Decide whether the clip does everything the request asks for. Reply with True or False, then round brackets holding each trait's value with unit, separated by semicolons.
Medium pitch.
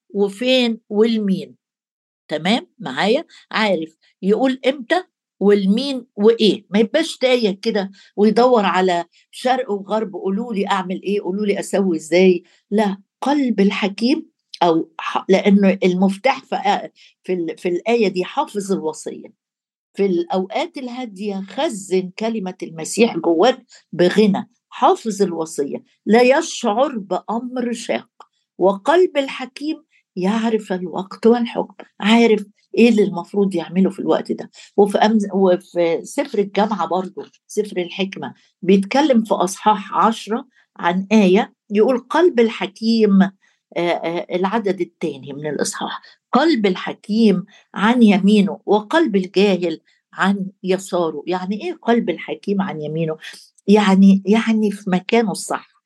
False (205 Hz)